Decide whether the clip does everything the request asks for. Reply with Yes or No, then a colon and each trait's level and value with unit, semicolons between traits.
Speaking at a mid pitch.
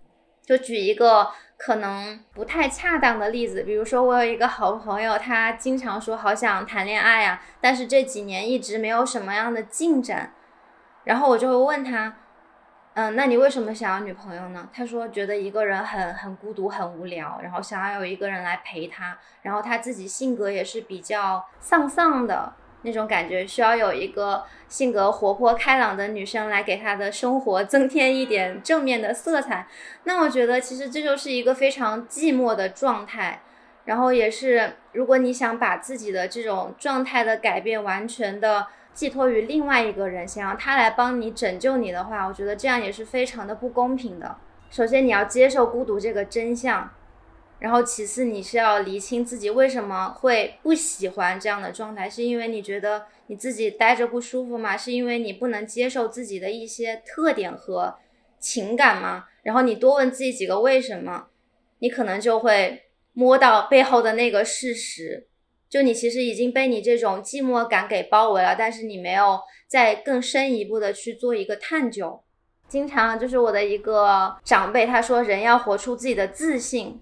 No: high, 230 Hz